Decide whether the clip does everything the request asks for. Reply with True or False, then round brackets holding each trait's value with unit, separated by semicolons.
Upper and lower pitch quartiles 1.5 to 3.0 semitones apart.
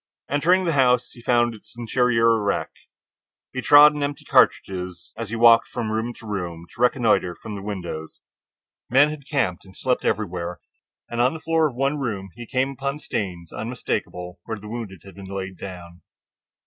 False (5.2 semitones)